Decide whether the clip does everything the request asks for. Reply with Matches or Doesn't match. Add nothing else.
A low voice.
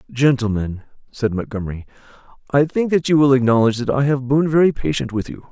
Matches